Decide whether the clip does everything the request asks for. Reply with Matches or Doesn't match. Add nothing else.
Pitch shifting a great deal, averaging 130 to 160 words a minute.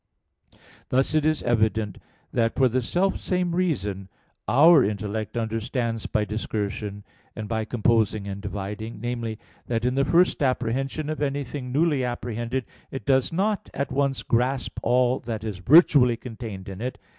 Doesn't match